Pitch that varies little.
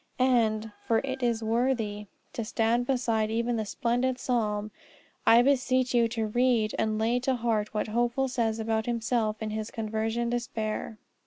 Yes: narrow, 2.0 semitones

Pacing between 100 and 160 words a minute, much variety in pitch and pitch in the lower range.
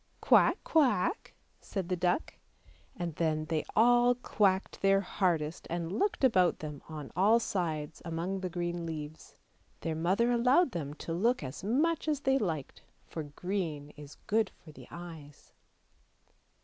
No: average, 155 wpm; wide, 5.9 semitones; medium, 175 Hz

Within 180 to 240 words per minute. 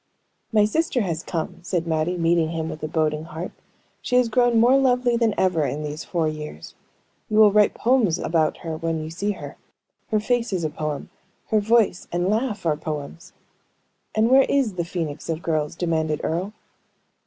Yes: average, 185 wpm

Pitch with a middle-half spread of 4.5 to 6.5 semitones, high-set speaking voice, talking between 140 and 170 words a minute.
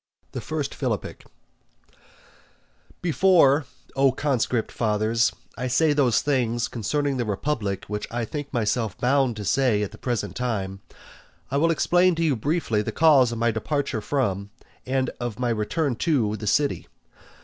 No: average, 4.8 semitones; low, 125 Hz; average, 145 wpm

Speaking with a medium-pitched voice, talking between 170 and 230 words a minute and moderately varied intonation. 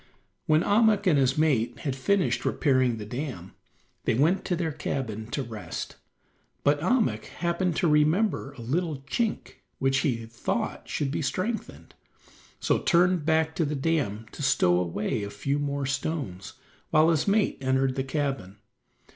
No: medium, 145 Hz; average, 155 wpm; average, 4.3 semitones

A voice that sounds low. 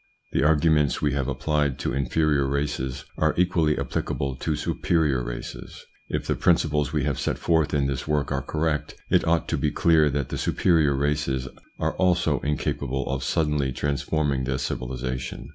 Yes: very low, 75 Hz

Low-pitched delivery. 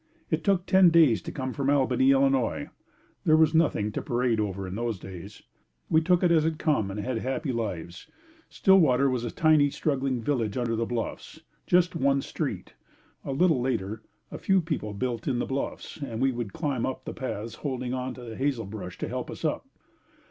Yes: low, 130 Hz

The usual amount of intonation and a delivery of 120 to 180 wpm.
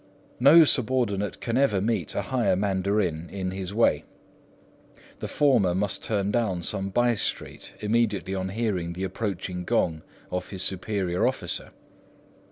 Yes: average, 3.8 semitones; average, 140 wpm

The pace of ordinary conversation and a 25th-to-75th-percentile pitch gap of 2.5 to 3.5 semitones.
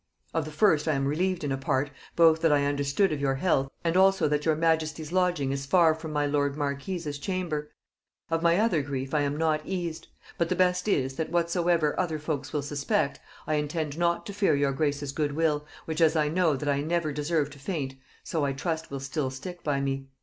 No: fast, 220 wpm; average, 3.0 semitones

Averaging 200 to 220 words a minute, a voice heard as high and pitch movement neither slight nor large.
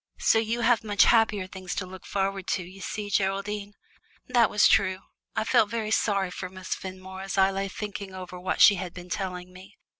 No: fast, 205 wpm; high, 195 Hz; narrow, 2.0 semitones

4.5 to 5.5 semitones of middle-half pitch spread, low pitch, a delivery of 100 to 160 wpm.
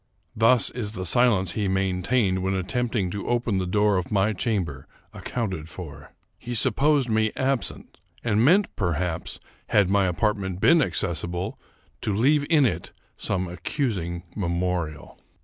Yes: average, 4.8 semitones; low, 100 Hz; average, 150 wpm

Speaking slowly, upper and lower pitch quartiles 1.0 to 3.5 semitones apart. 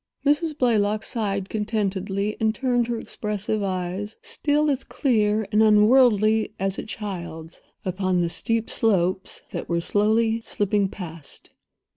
Yes: slow, 120 wpm; average, 2.8 semitones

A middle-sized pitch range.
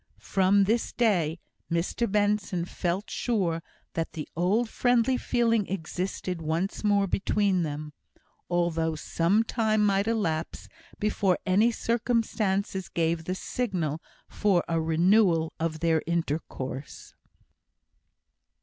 Yes: average, 4.3 semitones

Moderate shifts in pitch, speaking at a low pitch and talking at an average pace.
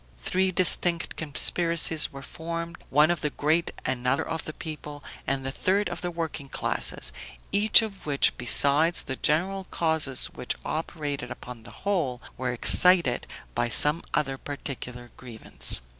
No: average, 4.2 semitones; medium, 150 Hz; average, 145 wpm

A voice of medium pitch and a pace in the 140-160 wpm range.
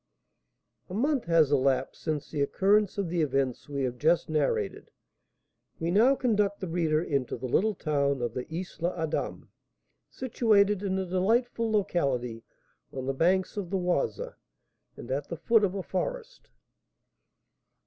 Yes: medium, 175 Hz; average, 150 wpm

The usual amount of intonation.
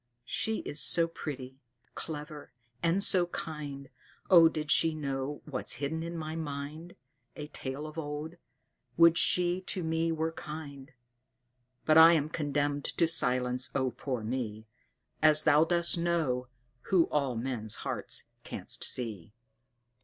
Yes: average, 3.3 semitones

